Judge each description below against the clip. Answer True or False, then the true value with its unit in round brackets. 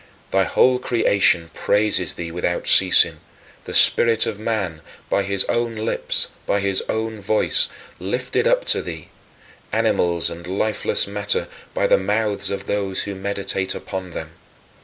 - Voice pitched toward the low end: True (100 Hz)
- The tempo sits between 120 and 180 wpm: True (145 wpm)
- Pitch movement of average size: False (2.3 semitones)